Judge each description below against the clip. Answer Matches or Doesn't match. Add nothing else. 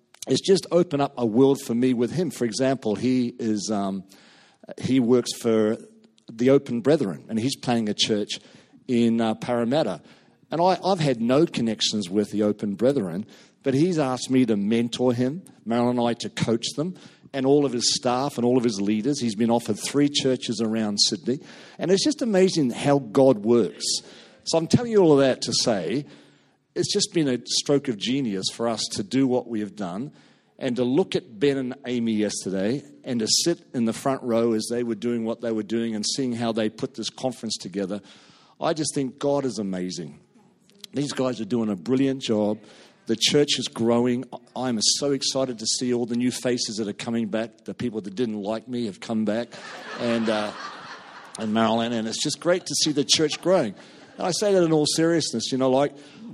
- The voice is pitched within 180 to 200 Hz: Doesn't match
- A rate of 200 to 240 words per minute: Matches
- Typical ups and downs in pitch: Matches